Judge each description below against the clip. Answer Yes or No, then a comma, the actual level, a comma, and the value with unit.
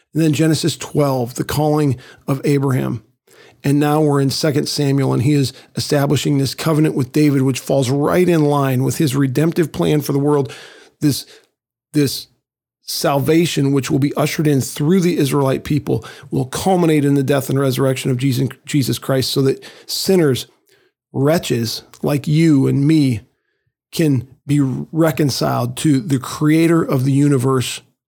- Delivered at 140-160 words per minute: Yes, average, 155 wpm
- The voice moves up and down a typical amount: No, narrow, 2.3 semitones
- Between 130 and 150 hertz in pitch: Yes, medium, 140 Hz